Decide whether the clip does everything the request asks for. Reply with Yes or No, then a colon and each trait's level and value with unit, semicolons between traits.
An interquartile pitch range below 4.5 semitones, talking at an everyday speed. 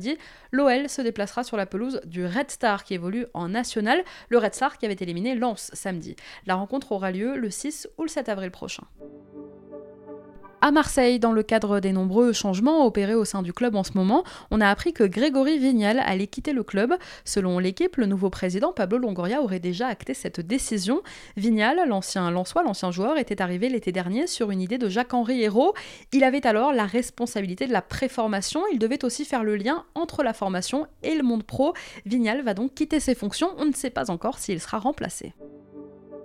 No: wide, 5.5 semitones; average, 200 wpm